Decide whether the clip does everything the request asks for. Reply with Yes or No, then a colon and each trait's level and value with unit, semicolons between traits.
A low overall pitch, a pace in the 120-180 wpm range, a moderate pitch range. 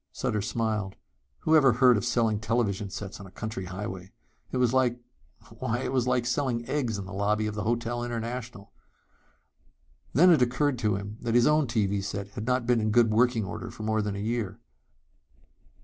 No: low, 115 Hz; average, 190 wpm; average, 3.0 semitones